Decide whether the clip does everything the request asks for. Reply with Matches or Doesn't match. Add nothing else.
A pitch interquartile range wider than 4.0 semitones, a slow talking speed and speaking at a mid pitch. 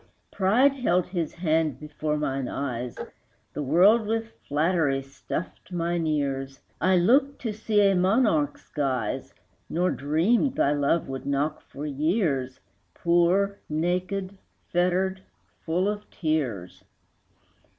Matches